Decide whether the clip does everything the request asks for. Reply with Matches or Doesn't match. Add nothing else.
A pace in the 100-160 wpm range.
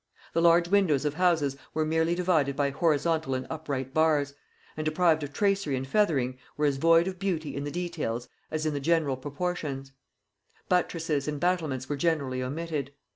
Doesn't match